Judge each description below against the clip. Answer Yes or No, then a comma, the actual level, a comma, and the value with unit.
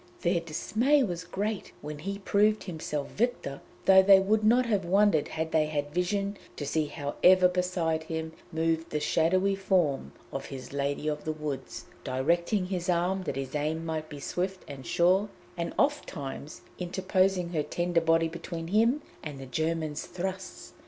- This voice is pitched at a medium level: Yes, medium, 170 Hz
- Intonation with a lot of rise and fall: No, average, 3.8 semitones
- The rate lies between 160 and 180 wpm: Yes, average, 170 wpm